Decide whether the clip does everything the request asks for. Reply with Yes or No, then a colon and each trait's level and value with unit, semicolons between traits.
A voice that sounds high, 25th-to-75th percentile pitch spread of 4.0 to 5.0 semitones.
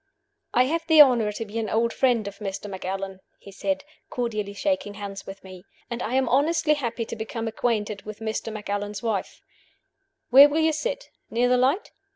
Yes: high, 225 Hz; average, 4.7 semitones